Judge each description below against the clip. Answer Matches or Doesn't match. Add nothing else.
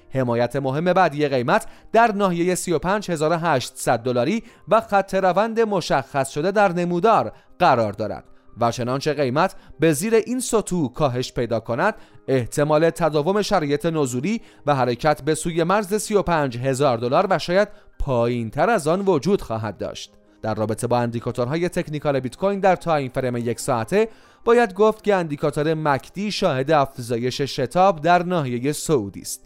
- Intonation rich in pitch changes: Matches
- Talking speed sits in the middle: Matches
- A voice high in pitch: Doesn't match